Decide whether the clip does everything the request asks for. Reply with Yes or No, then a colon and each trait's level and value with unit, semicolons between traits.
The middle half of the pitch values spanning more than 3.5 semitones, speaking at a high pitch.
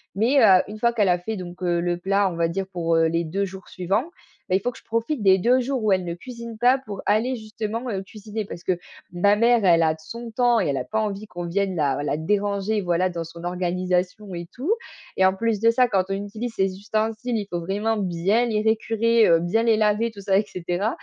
Yes: average, 4.0 semitones; high, 200 Hz